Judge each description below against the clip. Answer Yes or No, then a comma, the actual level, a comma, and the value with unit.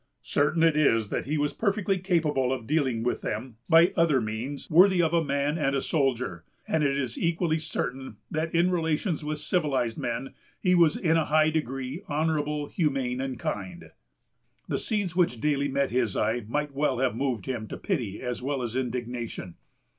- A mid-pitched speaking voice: Yes, medium, 145 Hz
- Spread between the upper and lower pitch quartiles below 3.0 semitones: No, average, 4.4 semitones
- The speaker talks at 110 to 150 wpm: No, average, 185 wpm